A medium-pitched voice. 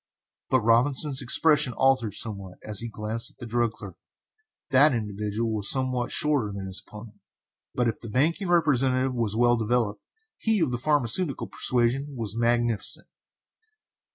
No: low, 120 Hz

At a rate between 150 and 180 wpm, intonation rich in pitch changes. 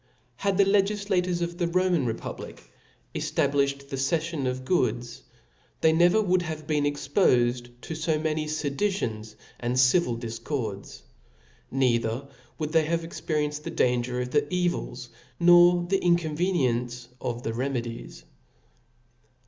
No: slow, 135 wpm; wide, 5.8 semitones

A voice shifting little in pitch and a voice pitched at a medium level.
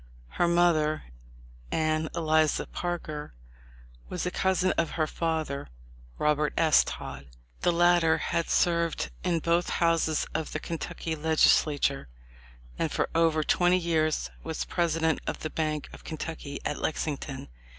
Yes: narrow, 1.7 semitones; medium, 160 Hz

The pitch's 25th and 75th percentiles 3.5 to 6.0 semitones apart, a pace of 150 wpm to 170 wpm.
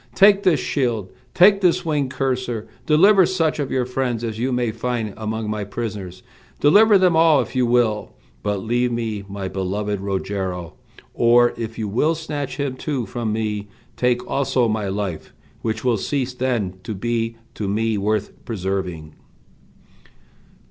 Yes: average, 4.2 semitones; average, 155 wpm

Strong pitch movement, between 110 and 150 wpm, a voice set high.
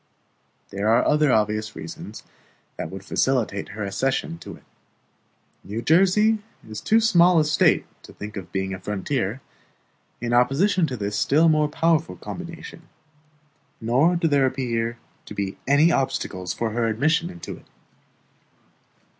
No: wide, 7.5 semitones; average, 145 wpm; low, 130 Hz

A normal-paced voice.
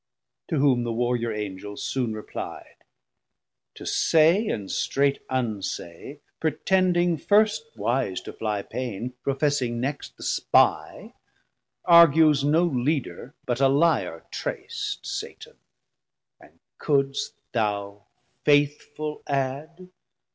No: slow, 105 wpm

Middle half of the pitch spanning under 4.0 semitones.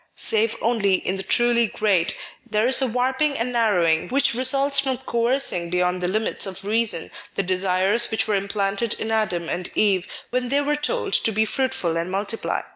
No: average, 4.8 semitones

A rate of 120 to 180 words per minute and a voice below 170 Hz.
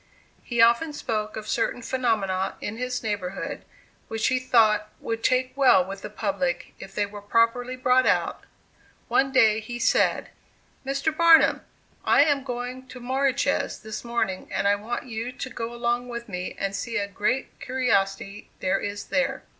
No: average, 165 wpm; high, 230 Hz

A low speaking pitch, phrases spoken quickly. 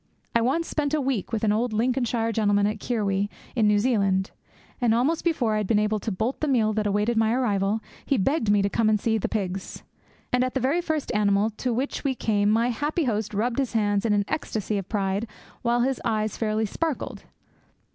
No: high, 220 Hz; fast, 215 wpm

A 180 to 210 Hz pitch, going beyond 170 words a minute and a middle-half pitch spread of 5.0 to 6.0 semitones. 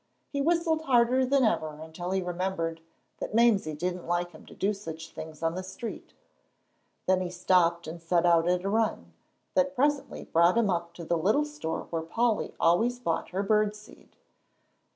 Yes: medium, 185 Hz; average, 180 wpm; wide, 5.5 semitones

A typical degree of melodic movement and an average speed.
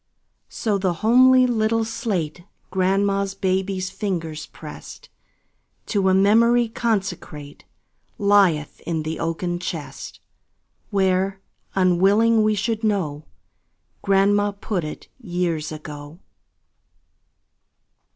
No: average, 3.8 semitones; slow, 95 wpm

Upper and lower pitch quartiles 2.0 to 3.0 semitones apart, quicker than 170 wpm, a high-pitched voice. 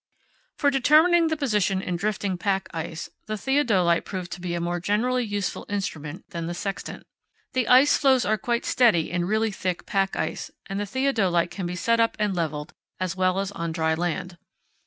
No: average, 4.8 semitones; average, 190 wpm; high, 195 Hz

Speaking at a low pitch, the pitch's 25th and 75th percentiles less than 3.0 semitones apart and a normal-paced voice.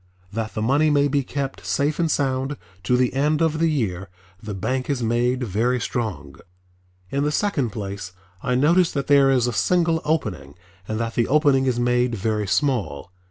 No: low, 130 Hz; average, 4.3 semitones; average, 185 wpm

